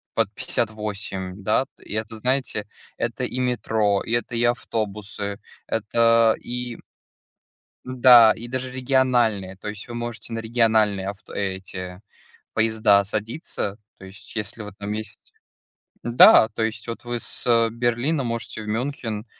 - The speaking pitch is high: No, low, 110 Hz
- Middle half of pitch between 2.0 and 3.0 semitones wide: Yes, narrow, 2.5 semitones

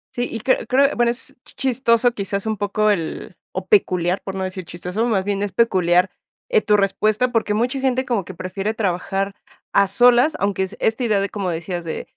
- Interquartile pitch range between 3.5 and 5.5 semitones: Yes, average, 4.1 semitones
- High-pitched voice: Yes, high, 205 Hz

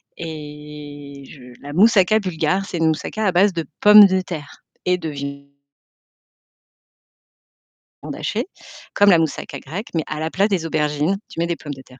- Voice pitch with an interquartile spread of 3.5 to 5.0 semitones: Yes, average, 4.2 semitones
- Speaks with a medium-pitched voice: Yes, medium, 160 Hz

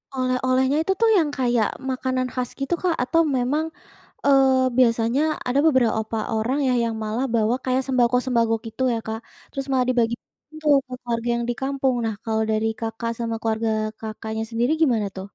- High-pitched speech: Yes, very high, 250 Hz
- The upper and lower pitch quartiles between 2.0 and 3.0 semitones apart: Yes, narrow, 2.6 semitones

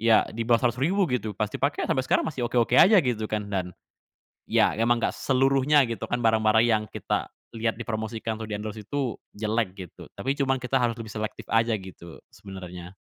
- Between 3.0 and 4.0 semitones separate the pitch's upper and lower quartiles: No, narrow, 2.6 semitones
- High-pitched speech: No, low, 115 Hz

